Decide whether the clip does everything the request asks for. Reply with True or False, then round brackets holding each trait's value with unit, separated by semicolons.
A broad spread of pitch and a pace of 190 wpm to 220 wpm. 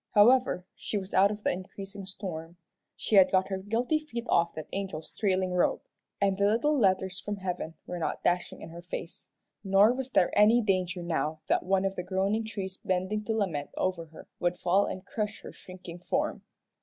False (2.6 semitones; 195 wpm)